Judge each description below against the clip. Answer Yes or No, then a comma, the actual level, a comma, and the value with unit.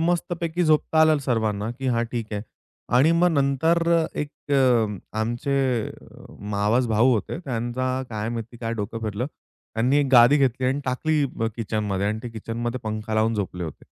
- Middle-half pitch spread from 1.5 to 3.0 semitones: No, average, 3.9 semitones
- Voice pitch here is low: Yes, low, 120 Hz